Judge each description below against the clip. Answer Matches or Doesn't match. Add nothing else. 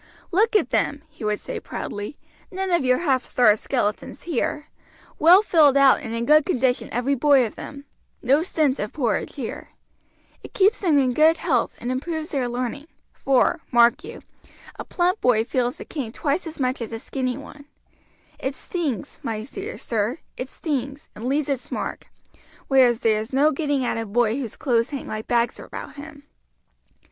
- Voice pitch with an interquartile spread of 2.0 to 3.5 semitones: Doesn't match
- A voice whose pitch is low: Doesn't match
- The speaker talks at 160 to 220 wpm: Matches